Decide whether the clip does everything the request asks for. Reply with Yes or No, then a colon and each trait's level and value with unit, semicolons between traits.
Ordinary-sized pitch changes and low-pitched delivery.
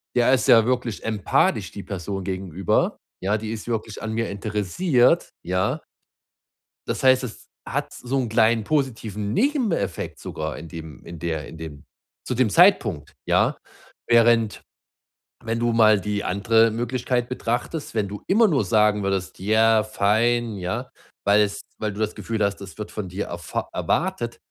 Yes: average, 3.2 semitones; low, 110 Hz